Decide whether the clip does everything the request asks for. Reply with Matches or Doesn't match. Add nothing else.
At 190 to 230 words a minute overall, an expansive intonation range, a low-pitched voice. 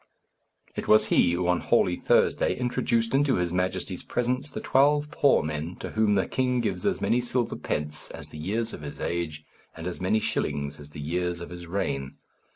Matches